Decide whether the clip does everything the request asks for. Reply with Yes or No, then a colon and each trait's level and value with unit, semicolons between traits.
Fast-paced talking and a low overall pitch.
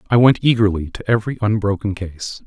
No: average, 170 wpm; low, 105 Hz